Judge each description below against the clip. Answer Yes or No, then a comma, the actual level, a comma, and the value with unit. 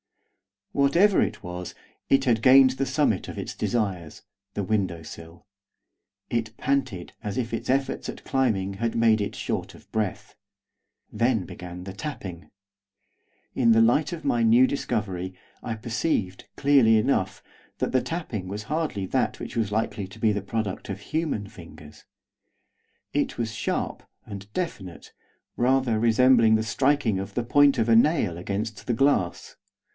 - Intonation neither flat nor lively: Yes, average, 4.9 semitones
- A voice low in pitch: Yes, low, 110 Hz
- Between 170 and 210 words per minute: No, average, 155 wpm